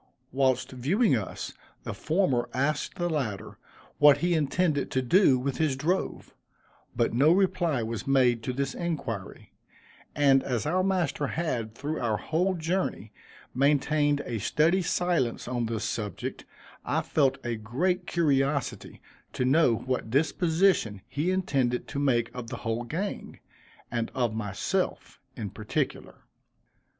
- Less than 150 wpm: Yes, average, 140 wpm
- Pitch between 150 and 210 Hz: No, medium, 140 Hz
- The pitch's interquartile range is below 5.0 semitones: No, wide, 5.4 semitones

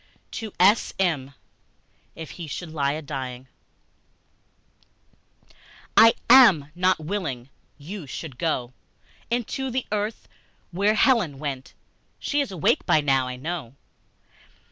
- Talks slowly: Yes, slow, 115 wpm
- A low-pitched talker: No, medium, 160 Hz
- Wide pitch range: Yes, wide, 7.1 semitones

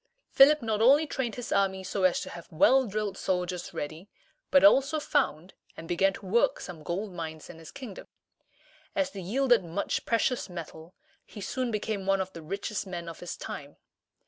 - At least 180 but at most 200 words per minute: Yes, average, 185 wpm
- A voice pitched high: Yes, high, 195 Hz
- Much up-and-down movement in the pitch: Yes, wide, 5.7 semitones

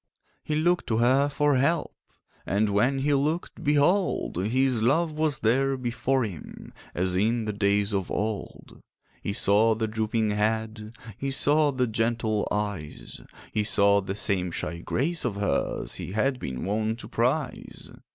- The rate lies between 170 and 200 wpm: No, average, 150 wpm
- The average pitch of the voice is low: Yes, low, 110 Hz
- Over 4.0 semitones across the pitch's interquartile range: Yes, average, 4.8 semitones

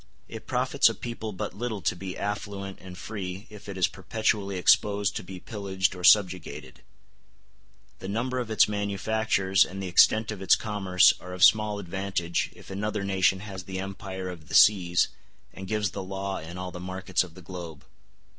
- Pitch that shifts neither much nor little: No, narrow, 2.1 semitones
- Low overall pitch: Yes, very low, 95 Hz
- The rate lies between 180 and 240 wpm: Yes, average, 185 wpm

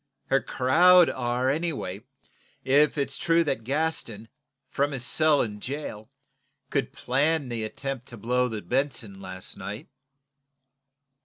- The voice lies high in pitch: No, low, 130 Hz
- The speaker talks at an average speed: No, slow, 130 wpm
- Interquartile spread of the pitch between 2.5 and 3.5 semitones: No, average, 4.6 semitones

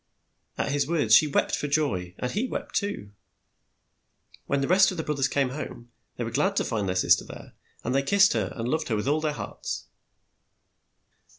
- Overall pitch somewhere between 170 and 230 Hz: No, medium, 140 Hz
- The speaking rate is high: Yes, fast, 210 wpm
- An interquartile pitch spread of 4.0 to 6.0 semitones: Yes, average, 5.2 semitones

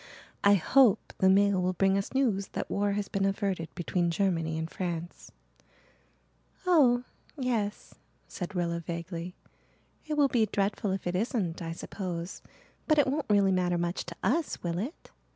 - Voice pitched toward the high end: Yes, high, 195 Hz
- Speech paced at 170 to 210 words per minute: No, average, 160 wpm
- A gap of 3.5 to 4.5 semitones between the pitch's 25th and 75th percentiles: Yes, average, 3.8 semitones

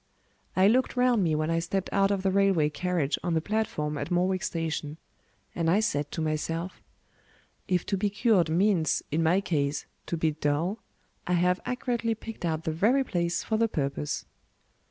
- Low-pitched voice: No, medium, 175 Hz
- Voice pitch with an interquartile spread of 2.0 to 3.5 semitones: No, average, 4.1 semitones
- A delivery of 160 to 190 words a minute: Yes, average, 180 wpm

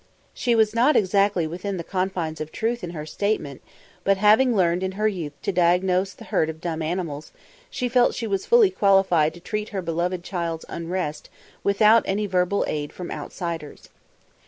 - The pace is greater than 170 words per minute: Yes, average, 180 wpm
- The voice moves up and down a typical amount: Yes, average, 3.7 semitones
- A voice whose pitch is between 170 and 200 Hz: Yes, medium, 185 Hz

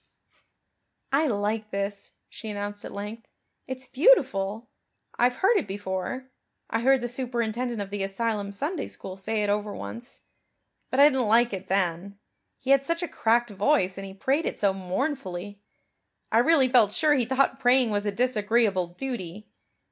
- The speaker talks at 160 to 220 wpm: Yes, average, 165 wpm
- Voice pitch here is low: No, high, 225 Hz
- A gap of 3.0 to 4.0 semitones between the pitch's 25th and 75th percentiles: No, average, 4.5 semitones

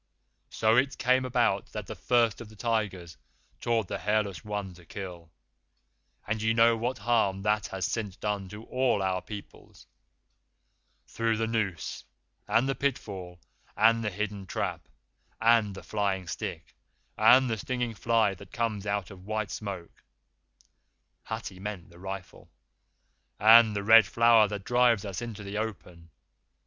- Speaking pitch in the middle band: No, low, 105 Hz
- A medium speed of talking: Yes, average, 150 wpm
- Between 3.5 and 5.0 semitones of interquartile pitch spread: No, average, 2.9 semitones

